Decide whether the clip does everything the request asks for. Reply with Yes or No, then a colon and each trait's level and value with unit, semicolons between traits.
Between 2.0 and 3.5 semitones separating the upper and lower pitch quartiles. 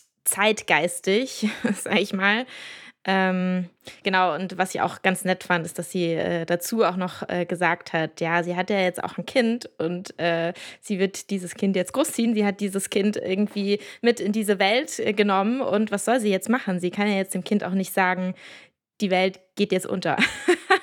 Yes: average, 2.7 semitones